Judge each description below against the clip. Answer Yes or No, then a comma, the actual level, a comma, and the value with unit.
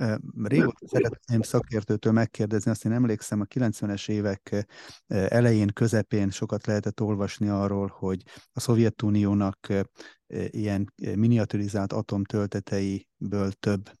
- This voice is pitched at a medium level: No, low, 105 Hz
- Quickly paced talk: No, slow, 100 wpm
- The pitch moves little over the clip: Yes, narrow, 1.9 semitones